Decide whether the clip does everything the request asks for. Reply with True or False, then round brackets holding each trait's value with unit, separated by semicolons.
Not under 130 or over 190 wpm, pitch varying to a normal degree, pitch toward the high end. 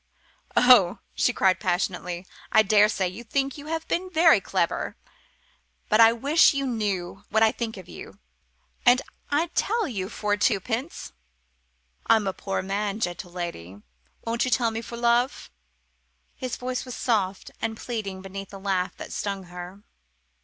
True (155 wpm; 4.6 semitones; 215 Hz)